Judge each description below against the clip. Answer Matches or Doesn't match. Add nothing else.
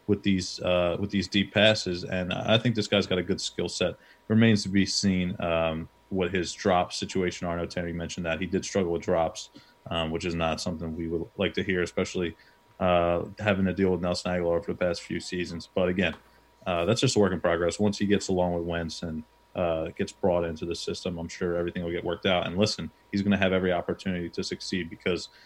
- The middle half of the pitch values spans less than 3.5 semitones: Matches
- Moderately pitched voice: Doesn't match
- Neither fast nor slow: Doesn't match